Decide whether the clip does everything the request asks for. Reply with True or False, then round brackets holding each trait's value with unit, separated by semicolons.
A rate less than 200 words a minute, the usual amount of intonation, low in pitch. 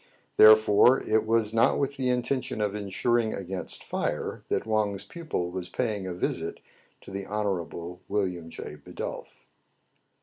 True (140 wpm; 3.5 semitones; 105 Hz)